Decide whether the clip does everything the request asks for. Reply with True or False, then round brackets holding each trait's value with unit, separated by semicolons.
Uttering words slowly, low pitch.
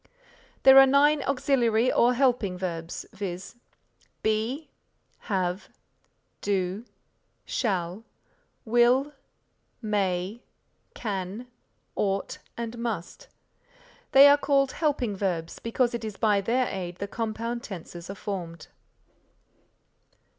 False (100 wpm; 220 Hz)